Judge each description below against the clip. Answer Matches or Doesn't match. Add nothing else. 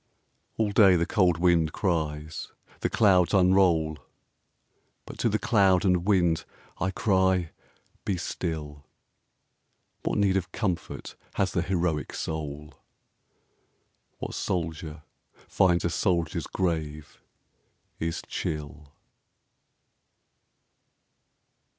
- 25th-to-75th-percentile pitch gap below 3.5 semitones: Matches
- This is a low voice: Matches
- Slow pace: Matches